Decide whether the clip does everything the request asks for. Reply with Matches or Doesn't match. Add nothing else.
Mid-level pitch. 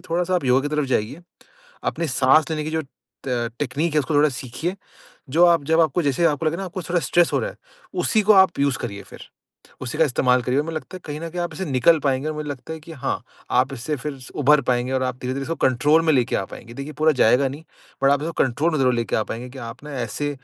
Matches